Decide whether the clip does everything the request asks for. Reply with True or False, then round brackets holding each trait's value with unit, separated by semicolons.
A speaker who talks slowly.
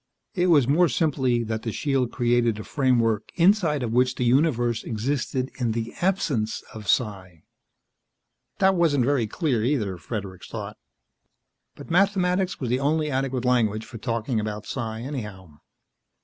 False (150 wpm)